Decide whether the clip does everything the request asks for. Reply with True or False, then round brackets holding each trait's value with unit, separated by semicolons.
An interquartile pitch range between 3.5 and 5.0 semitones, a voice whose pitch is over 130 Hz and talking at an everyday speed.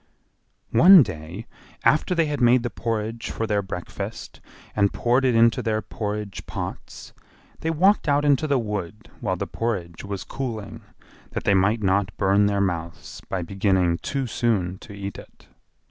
False (3.9 semitones; 105 Hz; 160 wpm)